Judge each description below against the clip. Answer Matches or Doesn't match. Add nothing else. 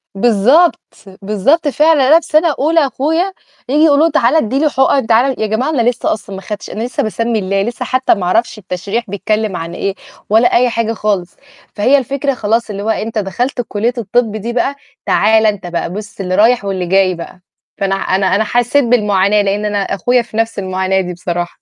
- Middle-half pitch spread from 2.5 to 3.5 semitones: Doesn't match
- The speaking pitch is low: Doesn't match